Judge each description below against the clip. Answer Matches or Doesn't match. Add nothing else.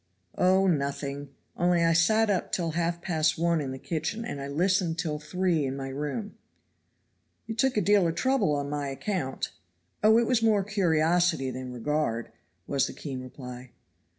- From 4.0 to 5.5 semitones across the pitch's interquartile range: Matches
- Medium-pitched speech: Matches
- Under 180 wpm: Matches